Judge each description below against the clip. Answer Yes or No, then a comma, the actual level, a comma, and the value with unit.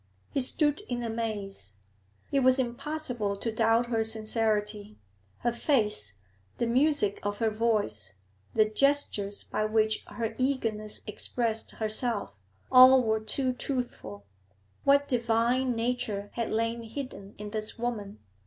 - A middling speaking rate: No, slow, 125 wpm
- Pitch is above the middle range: Yes, high, 225 Hz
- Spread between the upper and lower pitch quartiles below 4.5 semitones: Yes, average, 2.8 semitones